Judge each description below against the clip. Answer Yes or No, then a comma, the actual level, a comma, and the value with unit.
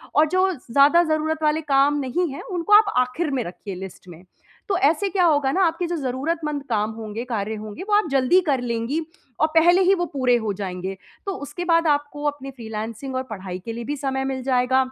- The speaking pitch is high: Yes, very high, 275 Hz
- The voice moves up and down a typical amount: No, wide, 5.7 semitones